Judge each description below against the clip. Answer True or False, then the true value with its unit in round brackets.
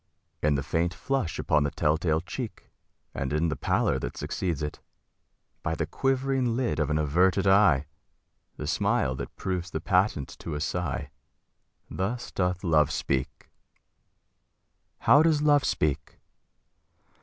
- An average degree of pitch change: False (5.9 semitones)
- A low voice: True (85 Hz)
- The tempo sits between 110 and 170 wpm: True (145 wpm)